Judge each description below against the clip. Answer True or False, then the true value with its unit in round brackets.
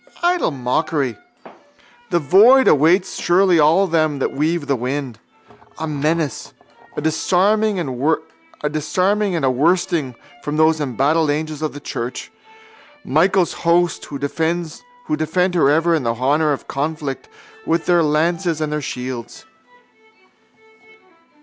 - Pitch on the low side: False (155 Hz)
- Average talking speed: False (120 wpm)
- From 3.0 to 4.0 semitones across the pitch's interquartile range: True (3.3 semitones)